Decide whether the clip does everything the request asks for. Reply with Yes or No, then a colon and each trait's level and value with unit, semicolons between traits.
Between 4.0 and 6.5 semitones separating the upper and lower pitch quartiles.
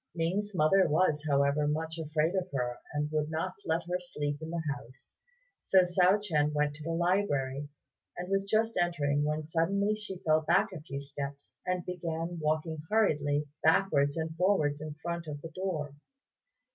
No: average, 3.4 semitones